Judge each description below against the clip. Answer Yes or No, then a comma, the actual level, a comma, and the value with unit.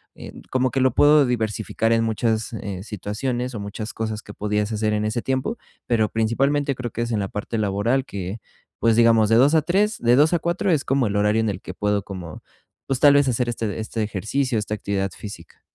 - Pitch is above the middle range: No, low, 115 Hz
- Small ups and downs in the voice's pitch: No, average, 3.8 semitones